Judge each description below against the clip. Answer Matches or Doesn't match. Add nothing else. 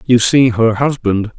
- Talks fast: Doesn't match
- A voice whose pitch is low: Matches